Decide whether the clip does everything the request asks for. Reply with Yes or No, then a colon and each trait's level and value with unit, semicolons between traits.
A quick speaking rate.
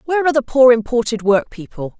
Yes: fast, 210 wpm